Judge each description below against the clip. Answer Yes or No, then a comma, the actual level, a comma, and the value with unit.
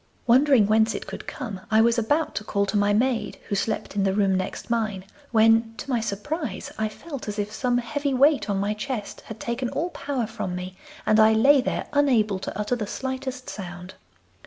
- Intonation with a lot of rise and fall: No, average, 4.1 semitones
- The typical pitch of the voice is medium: No, high, 225 Hz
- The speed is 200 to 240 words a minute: Yes, fast, 205 wpm